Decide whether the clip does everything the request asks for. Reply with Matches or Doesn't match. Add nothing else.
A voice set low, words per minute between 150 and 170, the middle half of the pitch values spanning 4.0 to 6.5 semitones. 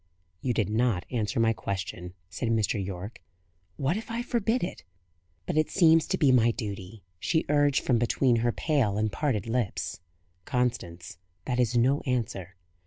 Matches